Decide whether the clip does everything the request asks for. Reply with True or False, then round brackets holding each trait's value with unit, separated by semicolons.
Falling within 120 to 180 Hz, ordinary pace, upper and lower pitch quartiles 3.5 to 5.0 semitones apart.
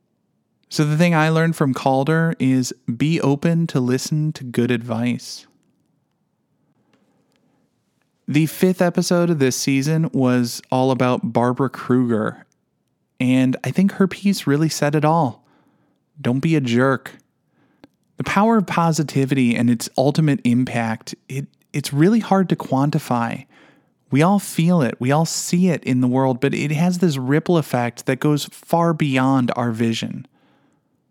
True (140 Hz; 145 wpm; 4.5 semitones)